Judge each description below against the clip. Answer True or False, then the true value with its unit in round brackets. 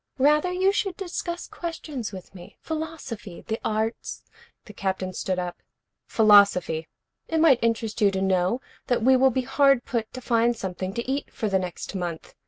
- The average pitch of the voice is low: False (230 Hz)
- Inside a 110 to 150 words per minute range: False (180 wpm)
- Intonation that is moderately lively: False (6.6 semitones)